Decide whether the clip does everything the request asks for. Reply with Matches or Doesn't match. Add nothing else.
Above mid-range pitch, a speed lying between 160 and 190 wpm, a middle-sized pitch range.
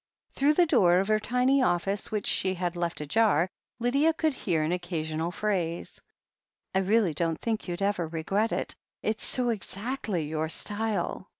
Matches